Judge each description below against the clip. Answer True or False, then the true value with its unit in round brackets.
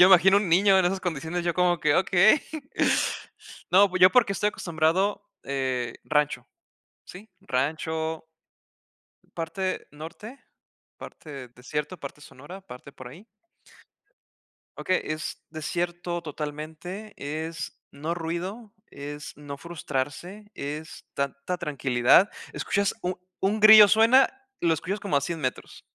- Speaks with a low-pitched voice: False (170 Hz)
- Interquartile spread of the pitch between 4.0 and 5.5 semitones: True (4.5 semitones)